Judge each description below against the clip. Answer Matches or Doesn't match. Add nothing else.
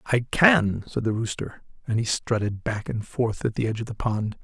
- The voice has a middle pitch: Doesn't match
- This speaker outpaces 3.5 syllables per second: Matches